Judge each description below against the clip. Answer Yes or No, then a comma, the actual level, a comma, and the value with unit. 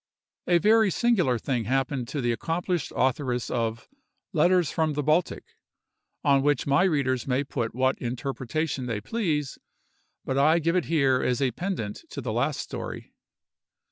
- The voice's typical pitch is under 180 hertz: Yes, medium, 140 Hz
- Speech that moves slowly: No, average, 155 wpm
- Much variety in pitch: No, average, 4.6 semitones